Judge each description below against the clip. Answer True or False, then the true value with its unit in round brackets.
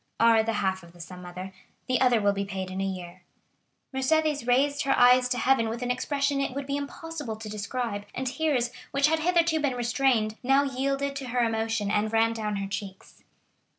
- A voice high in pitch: True (245 Hz)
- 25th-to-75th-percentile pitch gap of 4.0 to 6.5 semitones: True (4.9 semitones)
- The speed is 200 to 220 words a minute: True (205 wpm)